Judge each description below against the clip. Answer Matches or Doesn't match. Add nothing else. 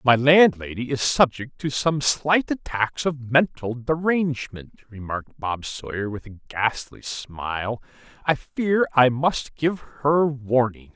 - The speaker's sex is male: Matches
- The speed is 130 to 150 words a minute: Matches